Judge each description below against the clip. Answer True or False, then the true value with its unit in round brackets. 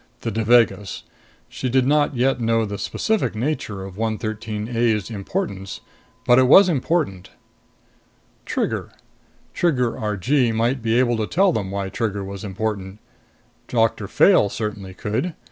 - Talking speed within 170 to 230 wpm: False (135 wpm)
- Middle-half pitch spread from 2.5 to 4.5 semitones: True (3.9 semitones)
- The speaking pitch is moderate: False (115 Hz)